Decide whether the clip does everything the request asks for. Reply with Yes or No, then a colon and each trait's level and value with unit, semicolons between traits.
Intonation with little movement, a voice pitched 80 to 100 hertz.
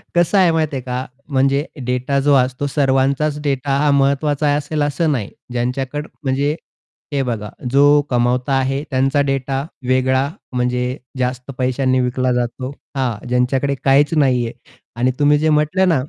No: narrow, 2.3 semitones; low, 135 Hz